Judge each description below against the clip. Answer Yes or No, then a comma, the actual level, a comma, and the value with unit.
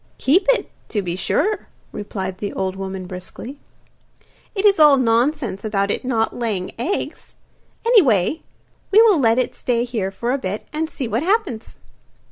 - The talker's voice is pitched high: Yes, high, 235 Hz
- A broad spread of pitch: Yes, wide, 7.5 semitones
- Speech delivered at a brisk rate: No, average, 160 wpm